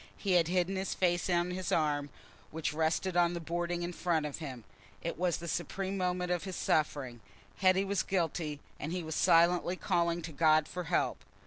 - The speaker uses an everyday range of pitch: No, narrow, 2.2 semitones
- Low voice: No, medium, 175 Hz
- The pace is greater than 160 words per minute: Yes, average, 195 wpm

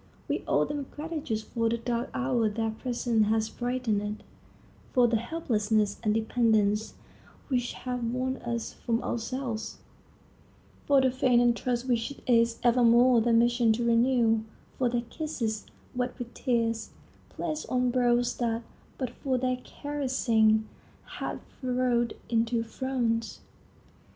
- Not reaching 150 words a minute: Yes, slow, 135 wpm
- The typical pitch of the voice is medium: No, high, 240 Hz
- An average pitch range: No, narrow, 2.0 semitones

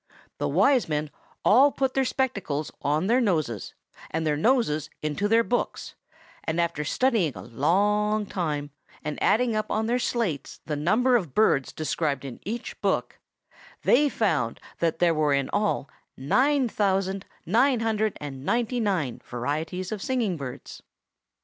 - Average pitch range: No, wide, 7.5 semitones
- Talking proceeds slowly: No, average, 150 wpm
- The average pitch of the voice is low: No, high, 190 Hz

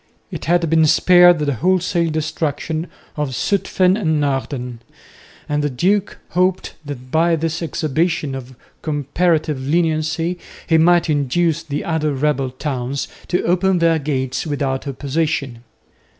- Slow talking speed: Yes, slow, 130 wpm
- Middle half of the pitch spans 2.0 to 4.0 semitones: Yes, average, 3.3 semitones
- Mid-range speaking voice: Yes, medium, 155 Hz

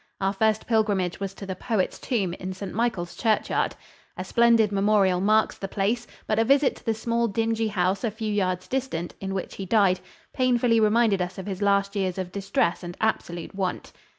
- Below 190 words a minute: No, average, 195 wpm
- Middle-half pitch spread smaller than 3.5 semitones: Yes, average, 3.1 semitones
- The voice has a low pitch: No, high, 200 Hz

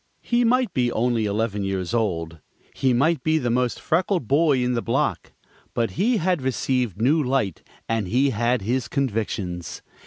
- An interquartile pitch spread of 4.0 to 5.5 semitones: Yes, average, 4.5 semitones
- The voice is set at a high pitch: No, low, 125 Hz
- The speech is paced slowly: No, average, 165 wpm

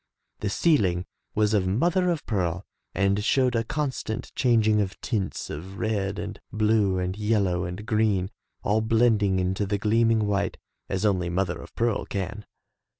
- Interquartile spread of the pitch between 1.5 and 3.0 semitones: Yes, average, 2.7 semitones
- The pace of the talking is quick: No, average, 160 wpm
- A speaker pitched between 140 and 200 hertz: No, low, 105 Hz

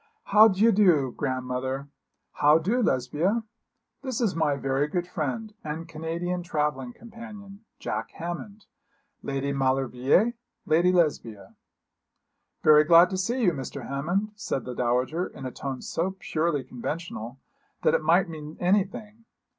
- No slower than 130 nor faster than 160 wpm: Yes, slow, 135 wpm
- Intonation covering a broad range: Yes, wide, 6.2 semitones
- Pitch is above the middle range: No, medium, 165 Hz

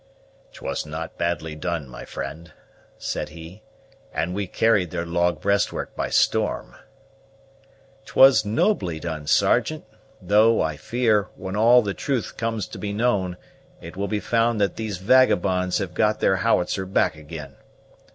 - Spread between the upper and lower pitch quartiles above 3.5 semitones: Yes, average, 4.3 semitones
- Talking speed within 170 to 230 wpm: No, average, 145 wpm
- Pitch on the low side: Yes, very low, 95 Hz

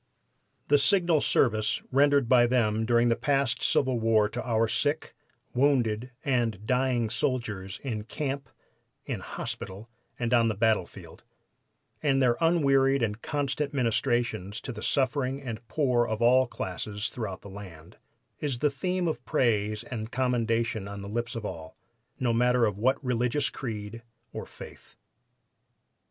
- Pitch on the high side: No, low, 120 Hz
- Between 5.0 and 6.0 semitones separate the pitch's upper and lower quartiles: No, average, 3.5 semitones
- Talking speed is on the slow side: No, average, 145 wpm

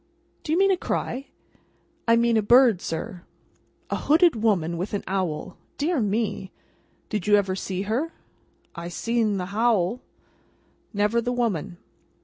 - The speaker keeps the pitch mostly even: No, average, 4.2 semitones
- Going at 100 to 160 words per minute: Yes, average, 145 wpm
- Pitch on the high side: Yes, high, 215 Hz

